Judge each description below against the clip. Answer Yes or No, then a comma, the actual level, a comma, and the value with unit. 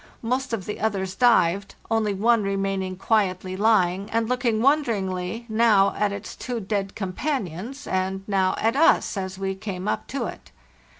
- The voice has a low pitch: No, high, 200 Hz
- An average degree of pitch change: Yes, average, 3.1 semitones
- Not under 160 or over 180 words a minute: Yes, average, 165 wpm